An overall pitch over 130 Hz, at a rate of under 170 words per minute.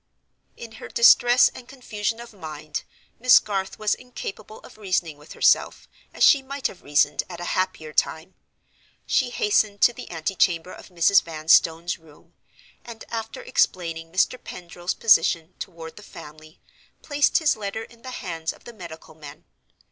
Yes: medium, 185 Hz; average, 155 wpm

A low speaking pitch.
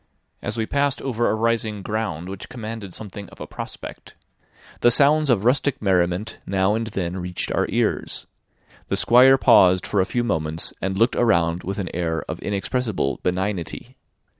Yes: low, 105 Hz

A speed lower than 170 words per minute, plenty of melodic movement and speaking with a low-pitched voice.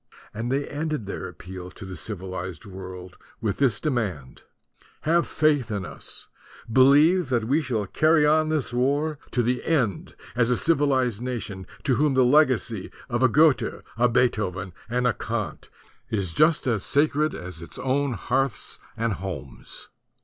Yes: average, 160 wpm; wide, 6.4 semitones; low, 125 Hz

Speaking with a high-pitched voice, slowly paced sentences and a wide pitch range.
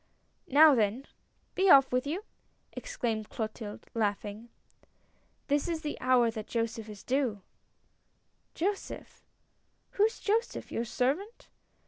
Yes: very high, 255 Hz; slow, 130 wpm; wide, 6.2 semitones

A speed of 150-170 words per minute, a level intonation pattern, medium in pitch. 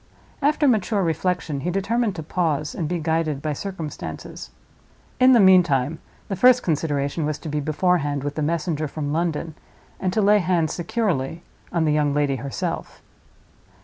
No: average, 160 wpm; average, 4.1 semitones; medium, 165 Hz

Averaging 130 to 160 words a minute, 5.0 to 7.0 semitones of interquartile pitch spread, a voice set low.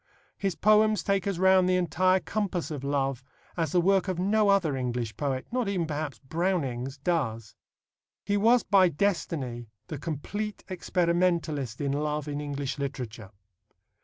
No: average, 150 wpm; wide, 5.5 semitones; medium, 165 Hz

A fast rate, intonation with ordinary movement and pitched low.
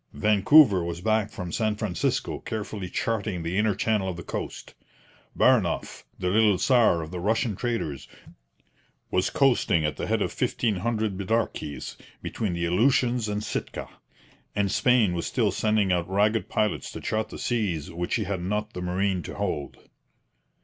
No: average, 165 wpm; average, 3.6 semitones; low, 100 Hz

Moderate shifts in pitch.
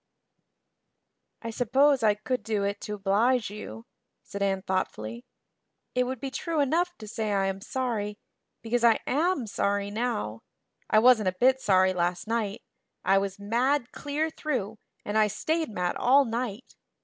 Yes: average, 4.3 semitones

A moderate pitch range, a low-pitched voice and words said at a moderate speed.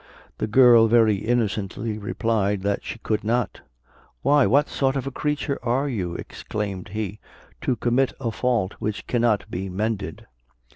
Yes: average, 3.4 semitones; low, 110 Hz; average, 150 wpm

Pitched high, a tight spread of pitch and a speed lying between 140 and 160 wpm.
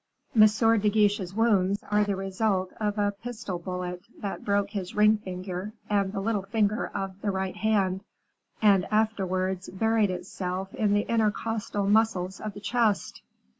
Yes: high, 205 Hz; narrow, 2.2 semitones; average, 155 wpm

